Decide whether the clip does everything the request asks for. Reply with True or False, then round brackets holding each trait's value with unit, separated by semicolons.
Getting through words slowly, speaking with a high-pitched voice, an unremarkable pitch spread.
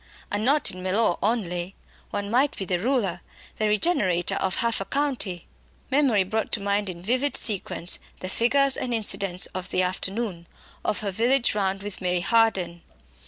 False (165 wpm; 200 Hz; 4.1 semitones)